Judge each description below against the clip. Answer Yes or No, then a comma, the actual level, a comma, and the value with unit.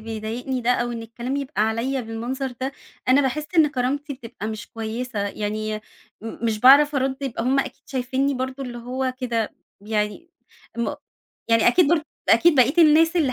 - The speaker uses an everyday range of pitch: Yes, average, 3.3 semitones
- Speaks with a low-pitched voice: No, very high, 255 Hz